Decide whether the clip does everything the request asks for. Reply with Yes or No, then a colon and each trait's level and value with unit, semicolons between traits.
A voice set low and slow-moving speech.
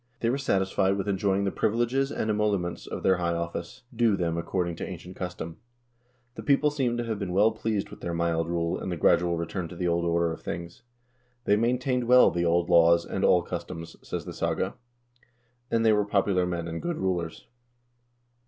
No: very low, 95 Hz; fast, 205 wpm